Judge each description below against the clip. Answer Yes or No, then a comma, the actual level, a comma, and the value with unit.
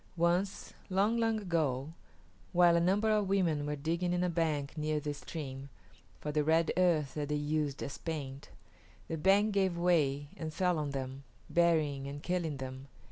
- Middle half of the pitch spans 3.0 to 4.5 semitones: Yes, average, 3.6 semitones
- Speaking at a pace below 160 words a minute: No, average, 175 wpm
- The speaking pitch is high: No, medium, 160 Hz